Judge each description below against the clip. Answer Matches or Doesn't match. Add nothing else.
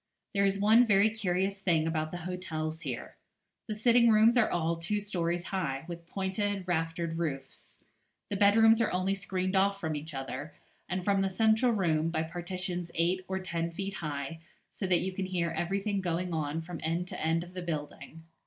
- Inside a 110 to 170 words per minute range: Doesn't match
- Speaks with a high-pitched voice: Doesn't match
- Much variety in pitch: Doesn't match